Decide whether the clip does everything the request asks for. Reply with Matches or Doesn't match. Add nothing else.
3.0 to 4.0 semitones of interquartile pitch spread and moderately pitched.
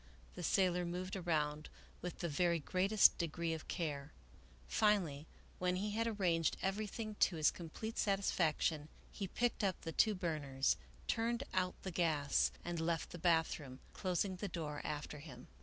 Matches